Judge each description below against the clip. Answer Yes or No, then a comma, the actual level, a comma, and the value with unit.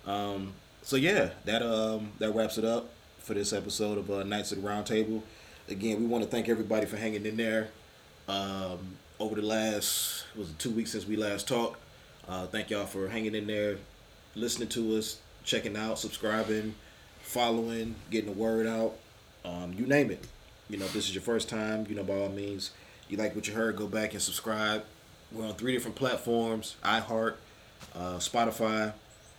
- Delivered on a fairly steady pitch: Yes, narrow, 1.6 semitones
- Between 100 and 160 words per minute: No, average, 190 wpm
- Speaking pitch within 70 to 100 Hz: No, low, 110 Hz